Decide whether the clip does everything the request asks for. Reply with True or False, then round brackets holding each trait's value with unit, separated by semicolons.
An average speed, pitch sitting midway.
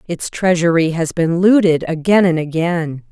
True (155 wpm; 170 Hz)